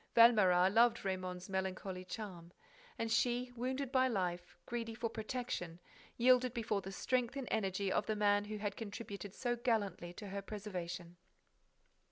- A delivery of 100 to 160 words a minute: Yes, average, 150 wpm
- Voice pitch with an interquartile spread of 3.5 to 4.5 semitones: Yes, average, 4.0 semitones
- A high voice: Yes, high, 210 Hz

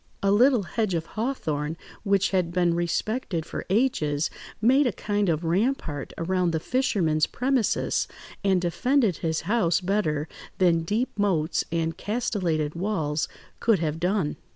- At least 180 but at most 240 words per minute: No, average, 140 wpm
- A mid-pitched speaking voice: Yes, medium, 180 Hz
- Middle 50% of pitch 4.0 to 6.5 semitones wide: Yes, average, 4.9 semitones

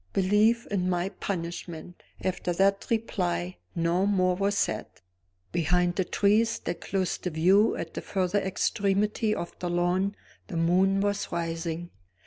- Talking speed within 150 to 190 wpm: No, average, 140 wpm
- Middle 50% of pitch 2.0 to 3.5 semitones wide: Yes, narrow, 2.6 semitones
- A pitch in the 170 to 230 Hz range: Yes, medium, 185 Hz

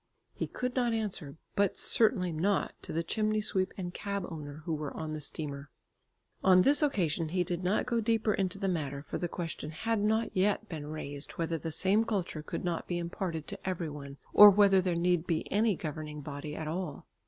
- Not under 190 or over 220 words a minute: Yes, fast, 205 wpm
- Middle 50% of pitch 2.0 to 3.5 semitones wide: No, average, 4.6 semitones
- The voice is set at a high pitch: No, medium, 180 Hz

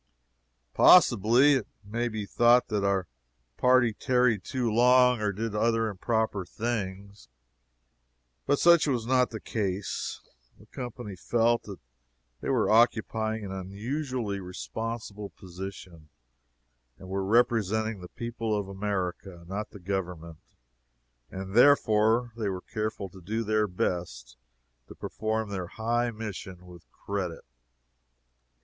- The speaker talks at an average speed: No, slow, 125 wpm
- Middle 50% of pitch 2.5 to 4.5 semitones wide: Yes, average, 3.5 semitones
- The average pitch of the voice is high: No, low, 105 Hz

